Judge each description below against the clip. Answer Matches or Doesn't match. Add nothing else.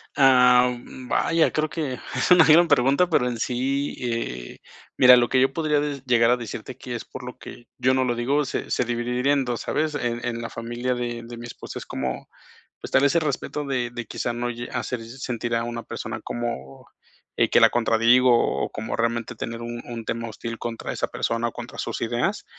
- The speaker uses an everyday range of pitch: Doesn't match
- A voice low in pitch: Matches